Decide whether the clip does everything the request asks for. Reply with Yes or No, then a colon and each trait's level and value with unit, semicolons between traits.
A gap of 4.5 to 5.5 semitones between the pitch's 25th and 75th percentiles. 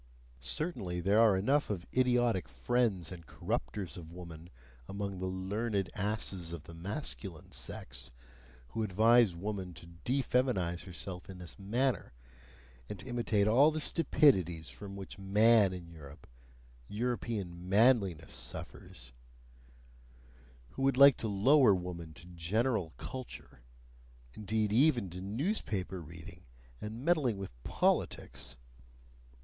Yes: average, 5.1 semitones